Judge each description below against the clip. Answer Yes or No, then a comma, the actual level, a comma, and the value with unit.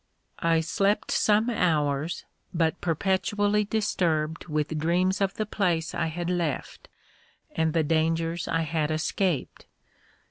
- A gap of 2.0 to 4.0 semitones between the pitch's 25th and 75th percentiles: Yes, average, 3.1 semitones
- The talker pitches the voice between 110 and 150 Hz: No, medium, 165 Hz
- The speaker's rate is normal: No, slow, 120 wpm